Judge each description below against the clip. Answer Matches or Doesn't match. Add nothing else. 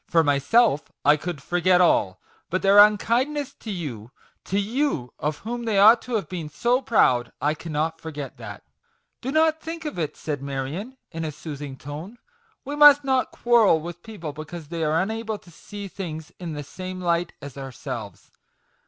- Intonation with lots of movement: Matches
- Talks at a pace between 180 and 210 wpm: Matches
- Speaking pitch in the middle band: Matches